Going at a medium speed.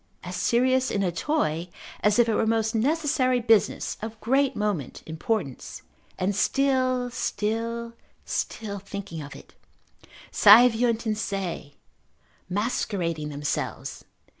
No: slow, 120 wpm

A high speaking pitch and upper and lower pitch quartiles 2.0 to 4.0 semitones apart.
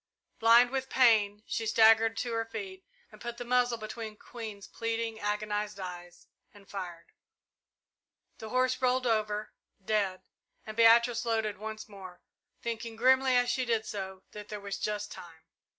Yes: high, 220 Hz; narrow, 2.4 semitones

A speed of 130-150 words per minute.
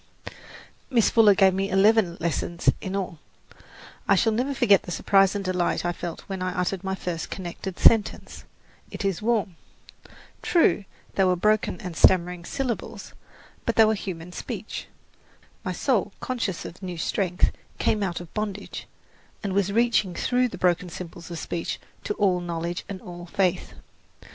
No: average, 160 wpm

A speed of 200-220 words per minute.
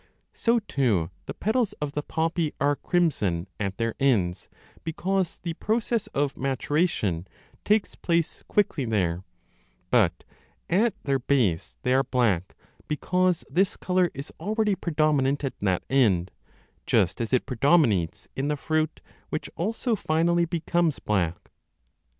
No: average, 140 wpm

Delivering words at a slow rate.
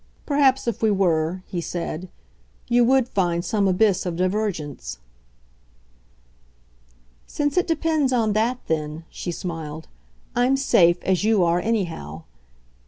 Yes: slow, 125 wpm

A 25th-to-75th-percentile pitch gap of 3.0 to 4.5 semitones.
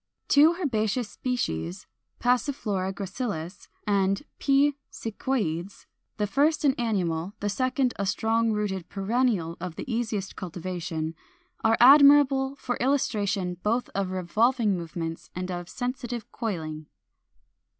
No: wide, 5.5 semitones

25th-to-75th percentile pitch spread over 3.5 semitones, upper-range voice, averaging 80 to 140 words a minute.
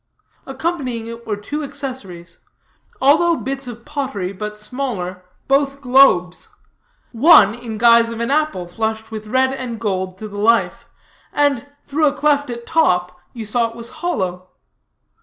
No: average, 4.8 semitones; high, 235 Hz; average, 150 wpm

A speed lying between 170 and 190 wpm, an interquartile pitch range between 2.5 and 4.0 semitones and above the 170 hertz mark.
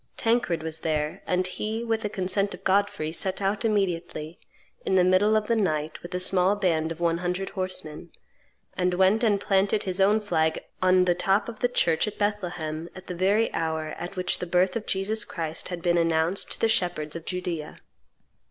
No: average, 200 wpm; average, 3.3 semitones; medium, 185 Hz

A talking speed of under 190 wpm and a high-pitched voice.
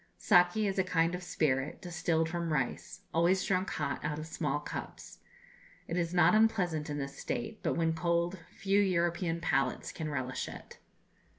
No: average, 170 wpm; medium, 170 Hz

